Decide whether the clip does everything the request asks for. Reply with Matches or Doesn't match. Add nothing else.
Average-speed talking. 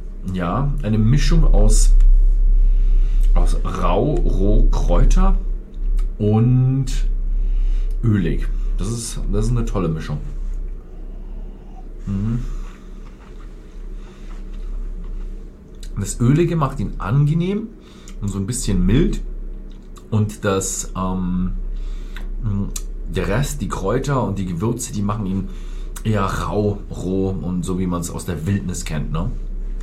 Doesn't match